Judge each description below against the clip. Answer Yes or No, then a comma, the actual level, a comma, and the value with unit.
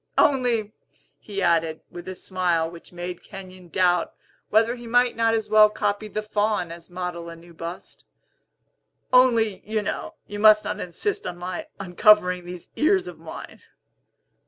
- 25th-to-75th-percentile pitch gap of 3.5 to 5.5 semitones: Yes, average, 3.9 semitones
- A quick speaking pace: No, average, 160 wpm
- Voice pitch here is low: No, high, 195 Hz